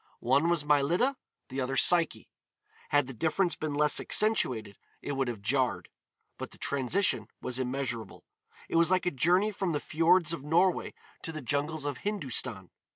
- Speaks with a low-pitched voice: No, medium, 145 Hz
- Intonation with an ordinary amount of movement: Yes, average, 4.8 semitones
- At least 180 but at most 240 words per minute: No, average, 165 wpm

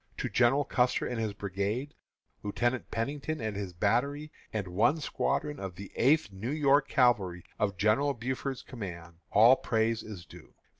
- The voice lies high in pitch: No, low, 115 Hz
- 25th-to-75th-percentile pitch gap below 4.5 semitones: No, average, 5.3 semitones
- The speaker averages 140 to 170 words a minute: Yes, average, 155 wpm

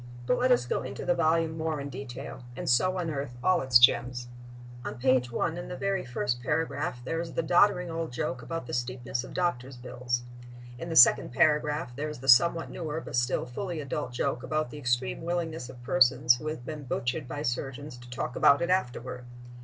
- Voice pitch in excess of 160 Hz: No, low, 135 Hz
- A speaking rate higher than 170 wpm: Yes, fast, 205 wpm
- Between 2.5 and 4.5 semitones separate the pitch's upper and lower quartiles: No, average, 4.9 semitones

